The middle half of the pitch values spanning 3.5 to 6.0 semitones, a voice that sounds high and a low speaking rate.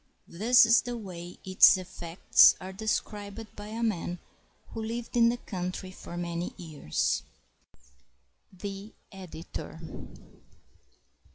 Yes: average, 4.0 semitones; high, 195 Hz; slow, 110 wpm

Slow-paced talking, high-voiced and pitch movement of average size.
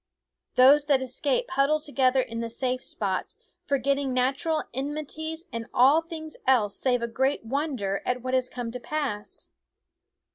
No: average, 155 wpm; very high, 265 Hz; average, 3.1 semitones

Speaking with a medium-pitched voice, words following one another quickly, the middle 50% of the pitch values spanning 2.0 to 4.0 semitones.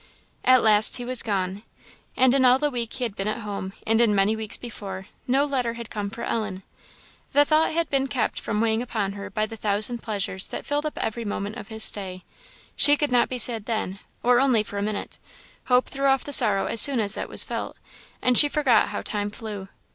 No: high, 225 Hz; fast, 225 wpm; average, 3.6 semitones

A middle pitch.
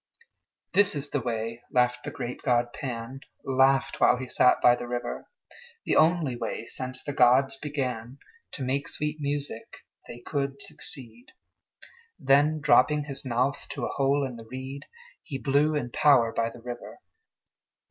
No: low, 130 Hz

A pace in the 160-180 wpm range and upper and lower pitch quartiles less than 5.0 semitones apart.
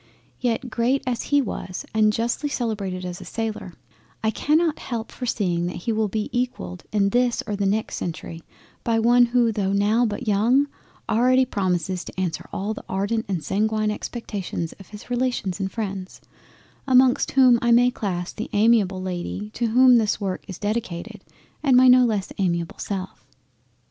Yes: average, 170 wpm; average, 4.1 semitones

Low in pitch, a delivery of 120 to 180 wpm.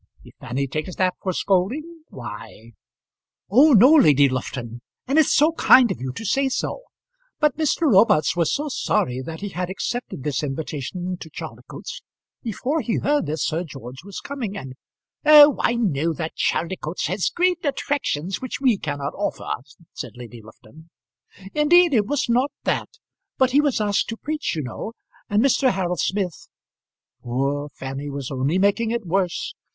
No: high, 190 Hz; average, 170 wpm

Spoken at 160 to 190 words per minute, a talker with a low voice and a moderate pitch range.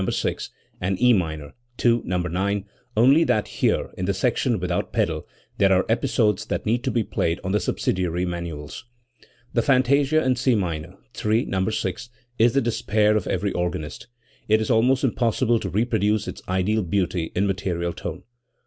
Yes: average, 170 wpm; low, 100 Hz; average, 4.6 semitones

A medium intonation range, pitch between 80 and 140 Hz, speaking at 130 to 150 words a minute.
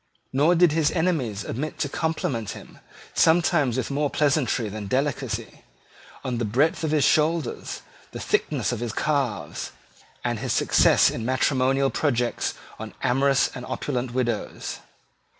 Yes: average, 4.0 semitones; low, 135 Hz; average, 140 wpm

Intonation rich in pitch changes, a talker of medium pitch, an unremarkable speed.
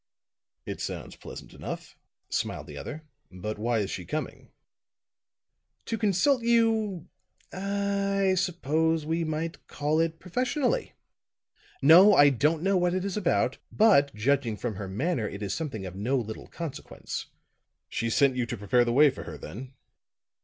Yes: wide, 8.1 semitones; medium, 155 Hz; average, 155 wpm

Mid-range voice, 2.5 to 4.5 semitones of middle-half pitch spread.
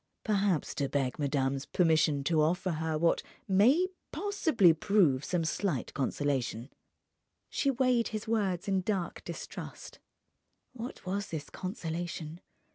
No: medium, 175 Hz; average, 5.1 semitones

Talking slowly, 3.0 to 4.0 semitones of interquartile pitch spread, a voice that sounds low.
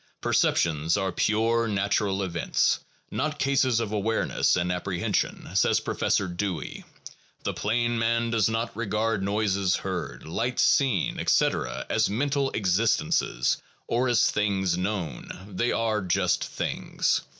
Yes: slow, 130 wpm; average, 3.6 semitones; low, 105 Hz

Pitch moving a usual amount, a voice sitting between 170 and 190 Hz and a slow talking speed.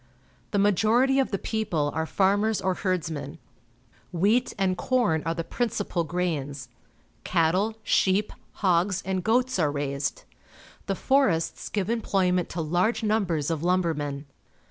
Yes: average, 4.7 semitones; medium, 185 Hz; slow, 130 wpm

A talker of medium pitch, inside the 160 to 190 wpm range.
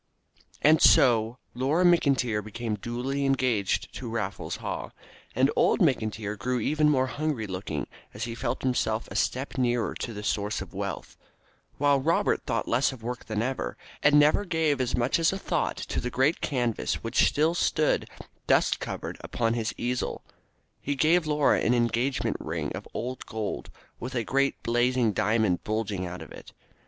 No: low, 125 Hz; average, 170 wpm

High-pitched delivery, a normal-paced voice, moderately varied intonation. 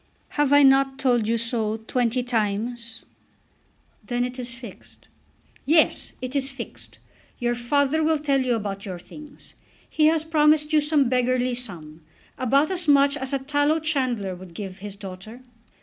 Yes: very high, 255 Hz; average, 160 wpm; average, 4.4 semitones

